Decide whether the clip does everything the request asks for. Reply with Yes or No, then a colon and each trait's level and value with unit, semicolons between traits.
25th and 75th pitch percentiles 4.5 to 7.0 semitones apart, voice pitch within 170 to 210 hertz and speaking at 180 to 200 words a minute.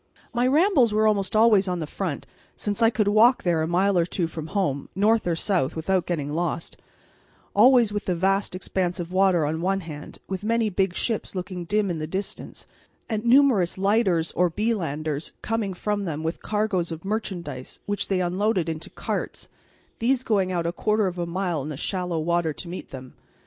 No: average, 3.9 semitones; medium, 185 Hz; average, 195 wpm